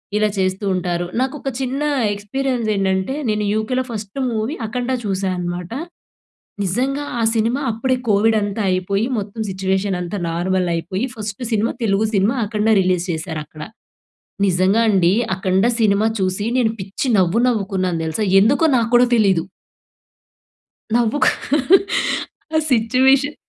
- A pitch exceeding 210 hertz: No, high, 205 Hz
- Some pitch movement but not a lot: Yes, average, 3.7 semitones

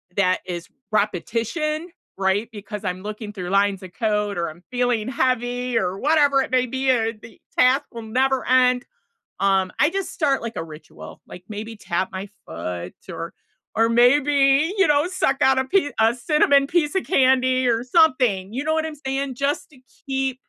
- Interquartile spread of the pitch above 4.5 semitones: Yes, average, 5.0 semitones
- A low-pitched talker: No, high, 245 Hz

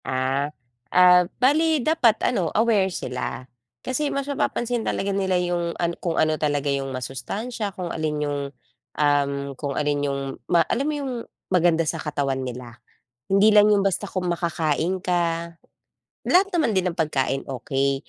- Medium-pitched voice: Yes, medium, 170 Hz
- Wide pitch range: Yes, wide, 6.3 semitones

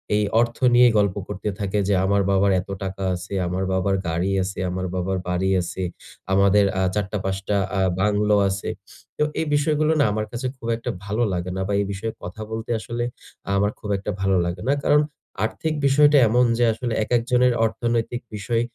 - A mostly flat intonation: No, average, 3.7 semitones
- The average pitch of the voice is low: Yes, low, 105 Hz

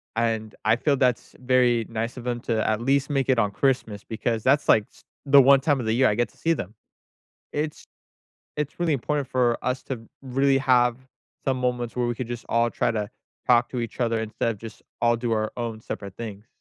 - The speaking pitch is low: Yes, low, 120 Hz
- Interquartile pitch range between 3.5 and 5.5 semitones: No, narrow, 2.6 semitones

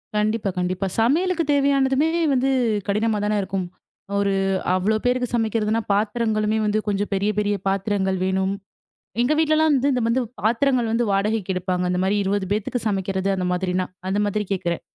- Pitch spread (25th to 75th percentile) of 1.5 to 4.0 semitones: Yes, average, 3.6 semitones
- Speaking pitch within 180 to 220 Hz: Yes, high, 210 Hz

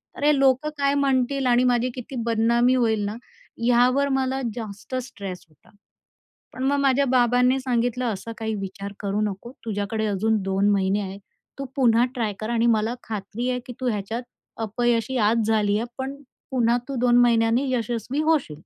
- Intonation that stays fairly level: No, average, 3.1 semitones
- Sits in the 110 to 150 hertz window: No, high, 235 Hz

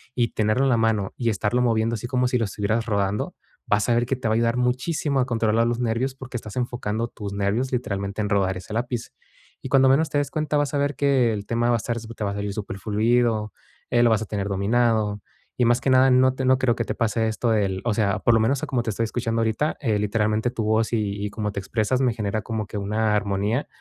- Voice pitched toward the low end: Yes, low, 115 Hz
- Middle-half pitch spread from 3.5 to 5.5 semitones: No, average, 2.9 semitones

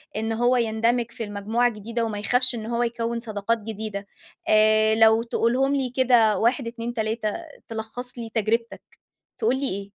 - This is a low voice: No, high, 230 Hz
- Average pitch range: No, narrow, 1.7 semitones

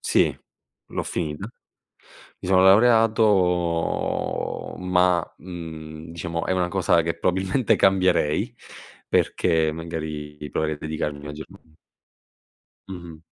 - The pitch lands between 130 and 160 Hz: No, very low, 85 Hz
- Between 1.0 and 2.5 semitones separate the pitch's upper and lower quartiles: No, average, 2.9 semitones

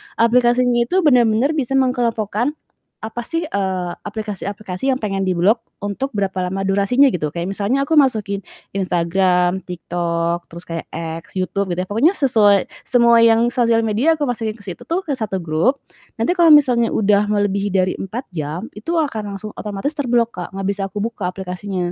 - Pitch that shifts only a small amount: No, average, 4.5 semitones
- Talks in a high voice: Yes, high, 210 Hz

